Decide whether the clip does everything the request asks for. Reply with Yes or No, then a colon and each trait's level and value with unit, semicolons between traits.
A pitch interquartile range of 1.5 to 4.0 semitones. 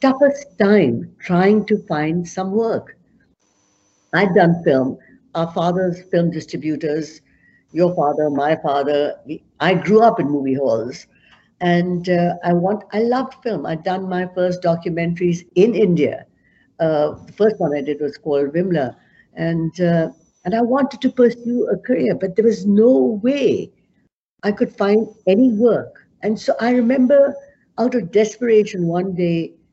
No: average, 5.1 semitones